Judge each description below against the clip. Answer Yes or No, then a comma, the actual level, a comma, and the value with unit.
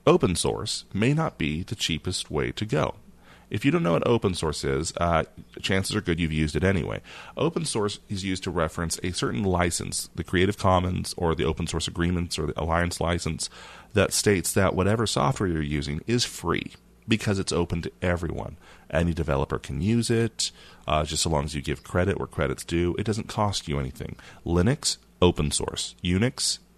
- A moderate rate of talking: Yes, average, 195 wpm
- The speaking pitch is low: Yes, very low, 85 Hz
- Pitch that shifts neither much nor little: Yes, average, 4.1 semitones